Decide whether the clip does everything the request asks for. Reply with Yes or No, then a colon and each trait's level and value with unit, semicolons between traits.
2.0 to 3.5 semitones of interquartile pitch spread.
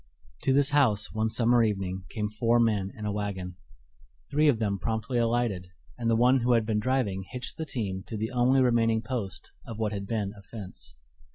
Yes: average, 3.0 semitones